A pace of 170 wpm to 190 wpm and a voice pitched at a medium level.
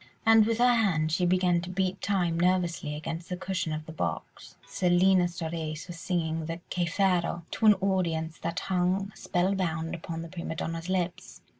Yes: average, 175 wpm; medium, 175 Hz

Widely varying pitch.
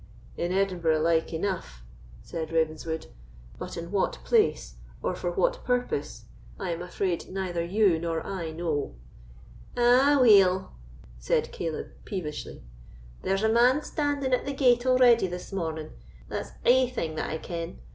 Yes: wide, 6.9 semitones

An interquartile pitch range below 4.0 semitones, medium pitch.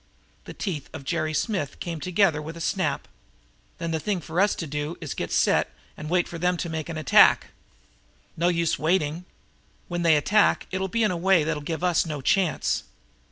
Yes: narrow, 2.6 semitones; medium, 170 Hz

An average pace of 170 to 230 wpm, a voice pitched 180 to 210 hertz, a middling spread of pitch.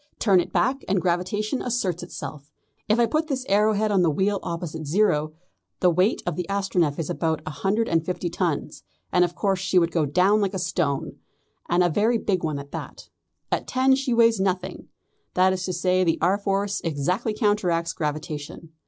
Yes: average, 195 wpm; medium, 185 Hz; average, 3.7 semitones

